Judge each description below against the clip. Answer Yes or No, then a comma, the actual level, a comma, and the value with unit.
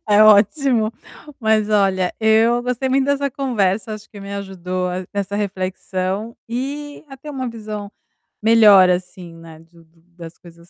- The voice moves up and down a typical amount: Yes, average, 4.1 semitones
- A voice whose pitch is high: Yes, high, 210 Hz